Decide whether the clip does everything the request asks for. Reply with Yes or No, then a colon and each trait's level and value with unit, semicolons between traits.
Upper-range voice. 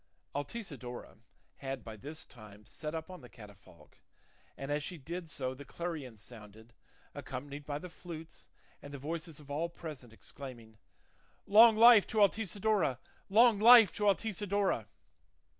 No: medium, 150 Hz